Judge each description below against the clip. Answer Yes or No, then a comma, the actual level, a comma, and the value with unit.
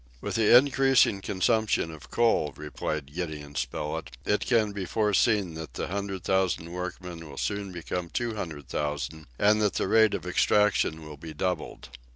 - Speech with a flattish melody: No, average, 4.8 semitones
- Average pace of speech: Yes, average, 165 wpm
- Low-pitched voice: Yes, very low, 90 Hz